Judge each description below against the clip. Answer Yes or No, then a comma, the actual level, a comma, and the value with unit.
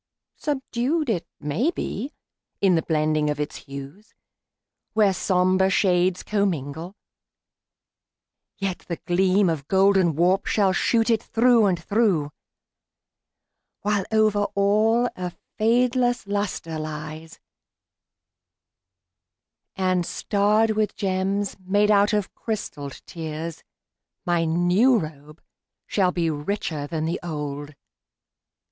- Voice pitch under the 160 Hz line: No, high, 190 Hz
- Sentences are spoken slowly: Yes, slow, 105 wpm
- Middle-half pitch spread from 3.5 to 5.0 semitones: Yes, average, 4.6 semitones